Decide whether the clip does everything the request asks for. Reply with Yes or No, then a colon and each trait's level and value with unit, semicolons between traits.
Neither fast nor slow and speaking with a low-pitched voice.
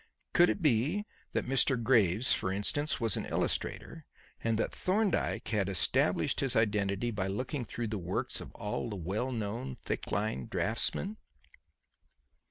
Yes: average, 150 wpm; low, 110 Hz